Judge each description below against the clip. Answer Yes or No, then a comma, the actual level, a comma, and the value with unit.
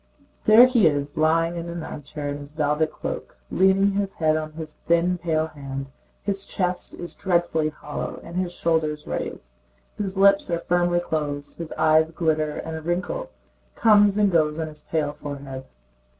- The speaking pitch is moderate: Yes, medium, 160 Hz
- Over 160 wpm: Yes, average, 175 wpm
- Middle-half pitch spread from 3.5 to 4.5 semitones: No, average, 3.0 semitones